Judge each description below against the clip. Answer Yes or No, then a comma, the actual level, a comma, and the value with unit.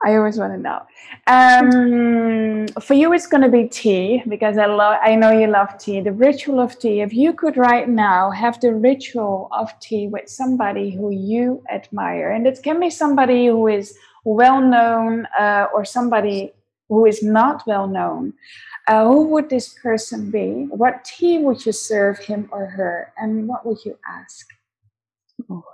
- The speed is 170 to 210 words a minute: Yes, average, 180 wpm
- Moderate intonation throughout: Yes, average, 3.5 semitones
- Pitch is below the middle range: No, high, 225 Hz